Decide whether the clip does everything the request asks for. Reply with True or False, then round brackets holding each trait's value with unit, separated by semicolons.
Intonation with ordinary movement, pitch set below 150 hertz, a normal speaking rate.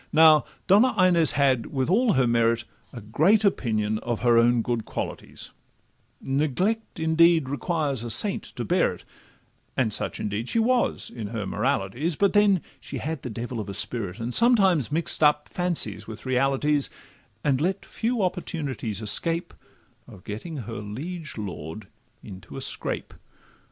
False (6.8 semitones; 135 Hz; 155 wpm)